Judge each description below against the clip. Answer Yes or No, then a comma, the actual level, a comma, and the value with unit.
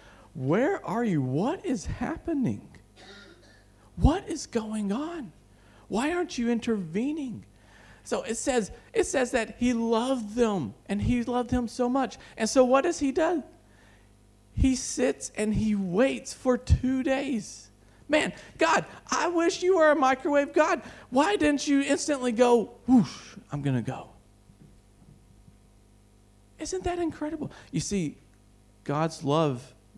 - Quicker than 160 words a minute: No, average, 140 wpm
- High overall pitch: Yes, high, 240 Hz